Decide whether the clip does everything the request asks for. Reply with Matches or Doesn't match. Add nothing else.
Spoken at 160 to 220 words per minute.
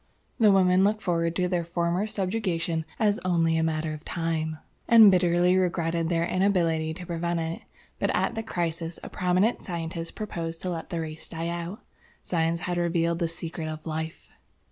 Matches